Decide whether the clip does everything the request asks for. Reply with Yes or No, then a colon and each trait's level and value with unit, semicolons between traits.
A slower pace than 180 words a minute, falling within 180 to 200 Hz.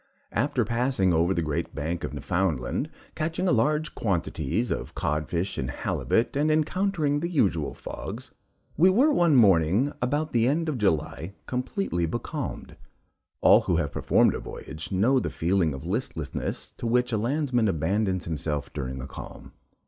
No: average, 155 wpm; low, 105 Hz